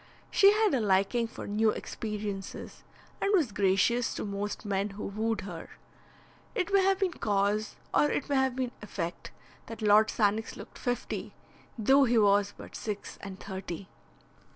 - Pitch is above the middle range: Yes, high, 215 Hz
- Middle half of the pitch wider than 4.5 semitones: No, average, 3.6 semitones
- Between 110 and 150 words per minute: No, average, 160 wpm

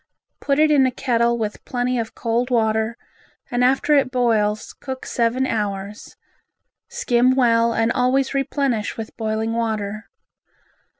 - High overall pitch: Yes, high, 235 Hz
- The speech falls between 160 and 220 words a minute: No, slow, 135 wpm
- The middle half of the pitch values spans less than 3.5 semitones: Yes, average, 2.7 semitones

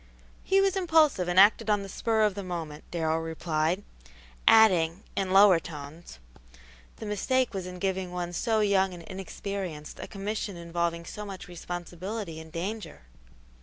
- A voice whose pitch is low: No, medium, 185 Hz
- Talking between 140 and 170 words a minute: Yes, average, 155 wpm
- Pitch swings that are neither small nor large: Yes, average, 3.6 semitones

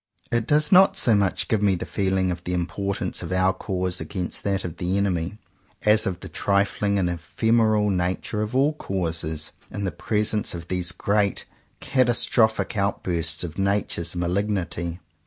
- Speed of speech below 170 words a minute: Yes, average, 160 wpm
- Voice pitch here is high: No, very low, 95 Hz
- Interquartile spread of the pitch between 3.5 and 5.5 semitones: No, average, 3.1 semitones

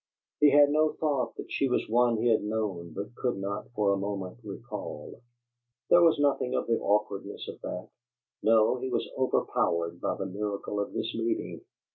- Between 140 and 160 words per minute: No, average, 180 wpm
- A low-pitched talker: Yes, low, 110 Hz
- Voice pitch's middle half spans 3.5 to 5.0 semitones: Yes, average, 4.1 semitones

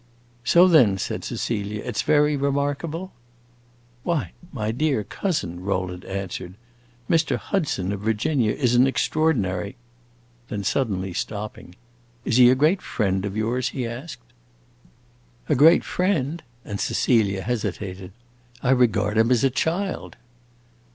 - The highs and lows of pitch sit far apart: Yes, wide, 6.8 semitones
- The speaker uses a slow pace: Yes, slow, 130 wpm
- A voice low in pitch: Yes, low, 115 Hz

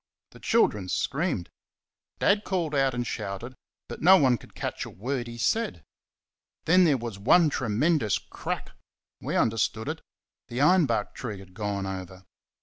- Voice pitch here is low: Yes, low, 120 Hz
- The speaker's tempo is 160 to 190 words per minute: No, average, 150 wpm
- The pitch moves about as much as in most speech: No, wide, 7.2 semitones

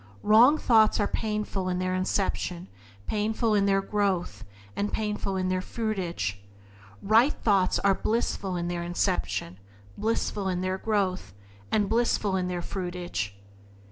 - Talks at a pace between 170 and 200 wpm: No, average, 140 wpm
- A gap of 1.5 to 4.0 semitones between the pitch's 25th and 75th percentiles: Yes, average, 2.8 semitones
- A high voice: Yes, high, 195 Hz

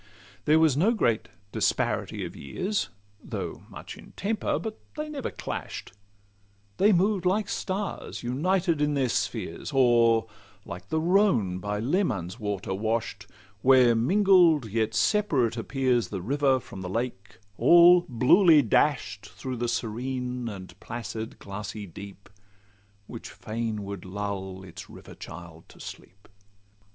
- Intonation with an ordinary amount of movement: No, wide, 7.8 semitones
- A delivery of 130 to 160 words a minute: Yes, slow, 135 wpm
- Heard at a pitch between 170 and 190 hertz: No, low, 120 Hz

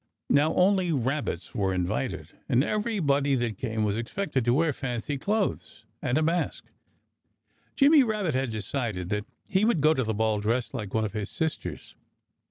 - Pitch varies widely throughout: Yes, wide, 7.1 semitones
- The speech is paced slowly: No, average, 170 wpm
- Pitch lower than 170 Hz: Yes, low, 135 Hz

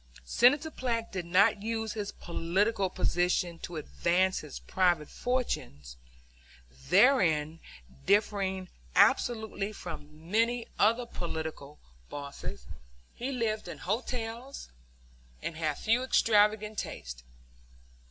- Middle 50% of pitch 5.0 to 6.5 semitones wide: Yes, wide, 5.5 semitones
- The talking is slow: Yes, slow, 100 wpm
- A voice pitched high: Yes, high, 200 Hz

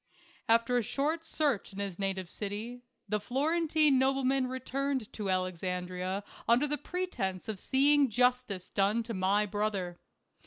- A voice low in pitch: No, high, 230 Hz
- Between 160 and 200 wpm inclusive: No, average, 140 wpm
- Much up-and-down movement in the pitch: Yes, wide, 5.7 semitones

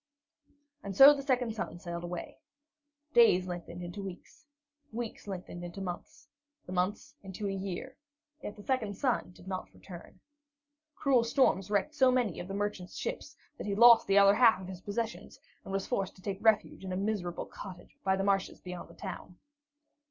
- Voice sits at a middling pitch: No, high, 195 Hz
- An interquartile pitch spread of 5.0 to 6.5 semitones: No, average, 3.8 semitones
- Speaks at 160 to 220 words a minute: Yes, average, 180 wpm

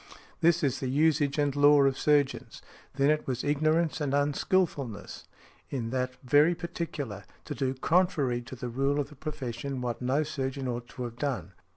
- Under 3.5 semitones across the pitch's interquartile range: Yes, average, 2.9 semitones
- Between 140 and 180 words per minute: Yes, average, 175 wpm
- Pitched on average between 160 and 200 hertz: No, medium, 140 Hz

